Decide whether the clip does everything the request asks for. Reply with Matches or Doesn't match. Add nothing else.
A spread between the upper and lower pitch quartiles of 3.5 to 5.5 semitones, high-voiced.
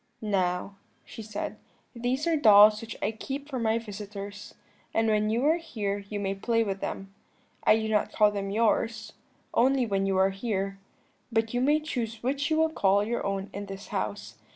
Doesn't match